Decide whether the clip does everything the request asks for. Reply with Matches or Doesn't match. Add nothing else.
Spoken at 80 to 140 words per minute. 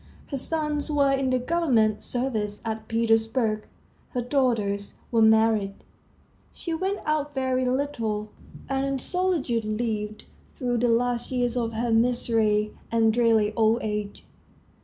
Matches